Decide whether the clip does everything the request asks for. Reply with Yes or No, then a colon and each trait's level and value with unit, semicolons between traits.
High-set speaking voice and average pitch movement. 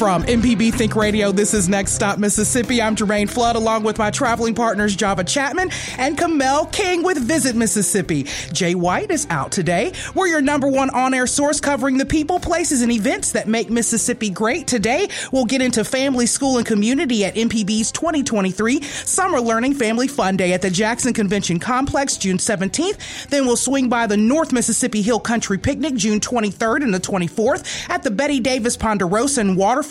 Yes: high, 235 Hz; average, 4.3 semitones